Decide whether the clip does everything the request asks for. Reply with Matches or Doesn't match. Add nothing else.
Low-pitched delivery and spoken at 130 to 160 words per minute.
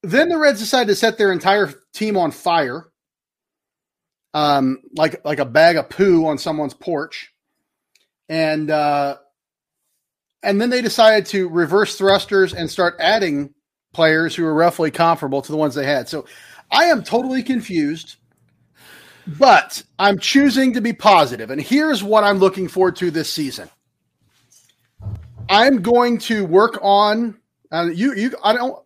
Doesn't match